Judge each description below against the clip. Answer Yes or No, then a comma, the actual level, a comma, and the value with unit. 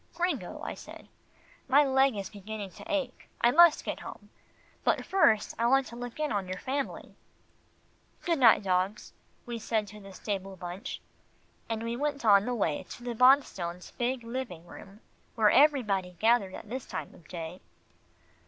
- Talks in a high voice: Yes, high, 225 Hz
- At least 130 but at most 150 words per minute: No, average, 170 wpm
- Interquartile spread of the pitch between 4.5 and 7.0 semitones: Yes, average, 5.2 semitones